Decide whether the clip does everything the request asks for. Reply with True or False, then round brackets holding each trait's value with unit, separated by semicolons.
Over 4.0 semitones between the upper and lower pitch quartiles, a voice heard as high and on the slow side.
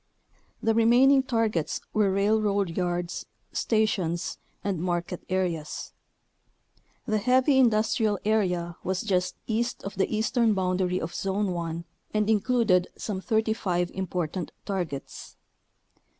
False (3.6 semitones; 195 Hz; 115 wpm)